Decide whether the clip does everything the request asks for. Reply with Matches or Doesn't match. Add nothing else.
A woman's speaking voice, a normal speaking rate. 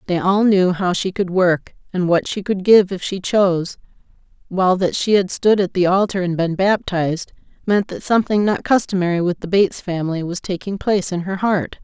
Doesn't match